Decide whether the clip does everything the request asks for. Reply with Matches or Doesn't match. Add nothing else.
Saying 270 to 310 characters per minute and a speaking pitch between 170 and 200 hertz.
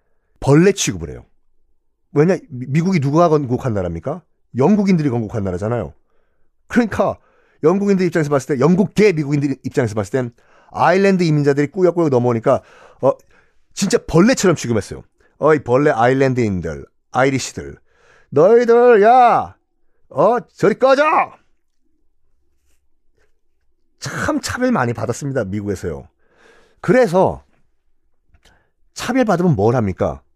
Doesn't match